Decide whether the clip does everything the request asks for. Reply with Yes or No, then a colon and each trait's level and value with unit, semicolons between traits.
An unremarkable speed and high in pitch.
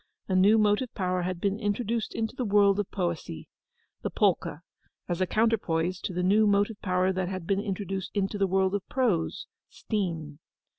Yes: average, 165 wpm; high, 195 Hz